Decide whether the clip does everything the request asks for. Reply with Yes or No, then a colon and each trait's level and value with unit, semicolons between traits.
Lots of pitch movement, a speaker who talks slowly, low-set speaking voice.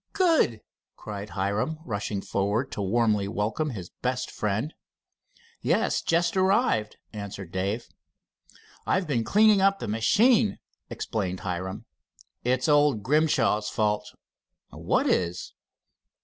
Yes: wide, 7.1 semitones; slow, 110 wpm; low, 110 Hz